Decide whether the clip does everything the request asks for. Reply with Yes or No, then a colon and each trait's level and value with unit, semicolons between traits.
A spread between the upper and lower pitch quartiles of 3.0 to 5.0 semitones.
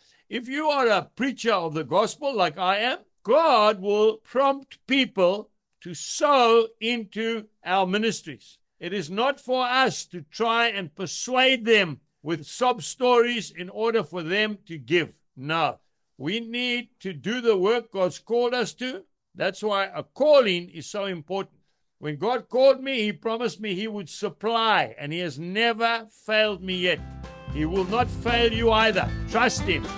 Yes: average, 4.5 semitones